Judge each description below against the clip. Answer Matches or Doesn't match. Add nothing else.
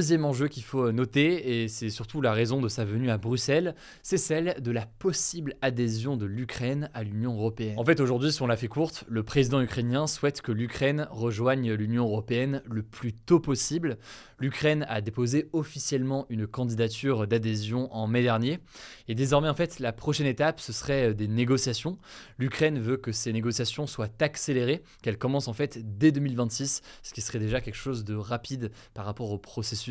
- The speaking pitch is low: Matches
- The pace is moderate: Matches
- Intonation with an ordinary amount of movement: Matches